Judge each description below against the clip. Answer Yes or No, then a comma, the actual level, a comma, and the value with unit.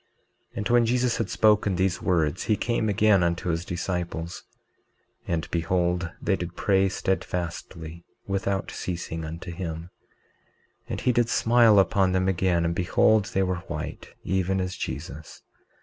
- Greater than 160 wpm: No, average, 150 wpm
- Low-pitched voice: Yes, very low, 90 Hz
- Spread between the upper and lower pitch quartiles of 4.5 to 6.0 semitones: No, narrow, 2.6 semitones